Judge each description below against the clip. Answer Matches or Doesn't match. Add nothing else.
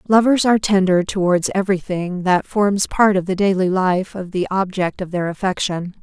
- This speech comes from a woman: Matches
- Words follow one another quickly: Doesn't match